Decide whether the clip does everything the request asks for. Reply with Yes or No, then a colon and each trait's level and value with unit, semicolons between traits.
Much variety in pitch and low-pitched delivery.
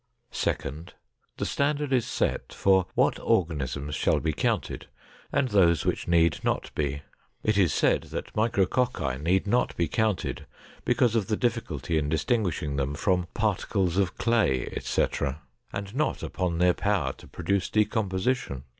Yes: wide, 6.0 semitones; very low, 95 Hz